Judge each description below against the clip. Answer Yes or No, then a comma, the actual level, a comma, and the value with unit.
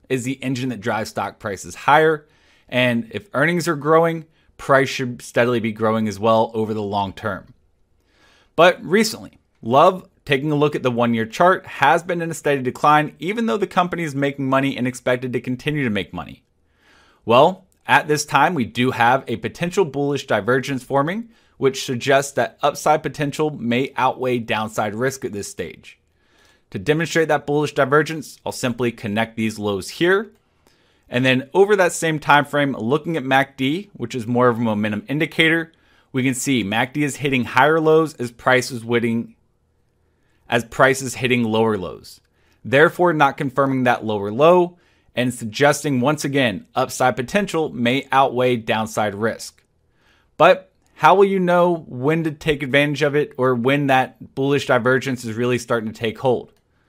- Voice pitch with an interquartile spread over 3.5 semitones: Yes, average, 4.1 semitones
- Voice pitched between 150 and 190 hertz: No, low, 135 Hz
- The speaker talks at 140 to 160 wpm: No, average, 170 wpm